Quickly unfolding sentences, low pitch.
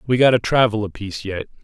Yes: fast, 220 wpm; low, 110 Hz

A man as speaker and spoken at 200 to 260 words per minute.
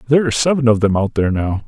No: male; fast, 285 wpm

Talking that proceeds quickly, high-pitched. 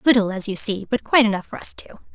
Yes: fast, 280 wpm; high, 215 Hz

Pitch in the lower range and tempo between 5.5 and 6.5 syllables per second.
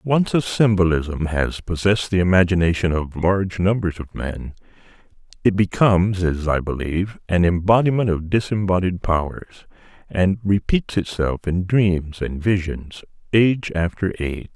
No: very low, 90 Hz; 4.6 syllables/s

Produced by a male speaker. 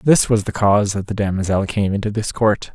Yes: male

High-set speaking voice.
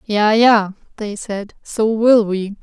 Yes: high, 210 Hz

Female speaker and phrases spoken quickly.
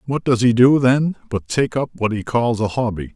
No: male; fast, 245 wpm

